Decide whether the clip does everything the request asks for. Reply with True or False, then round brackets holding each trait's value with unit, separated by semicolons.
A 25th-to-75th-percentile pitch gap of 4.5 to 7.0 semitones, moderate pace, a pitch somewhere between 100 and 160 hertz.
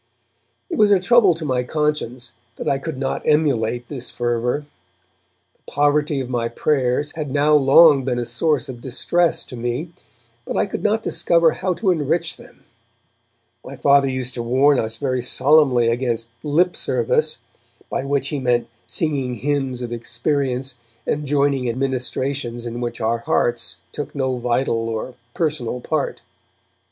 False (3.6 semitones; 160 wpm; 135 Hz)